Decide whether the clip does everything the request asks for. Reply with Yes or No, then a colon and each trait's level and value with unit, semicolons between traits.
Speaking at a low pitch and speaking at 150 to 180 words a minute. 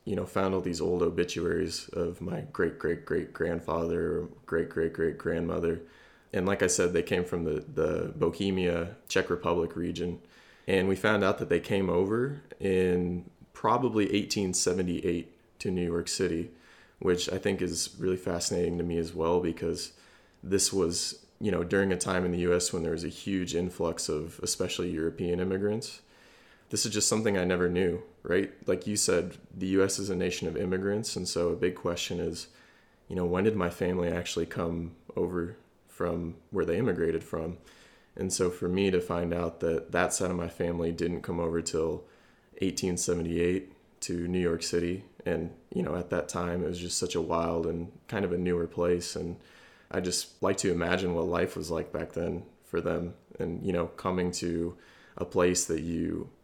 No: very low, 90 Hz; average, 190 wpm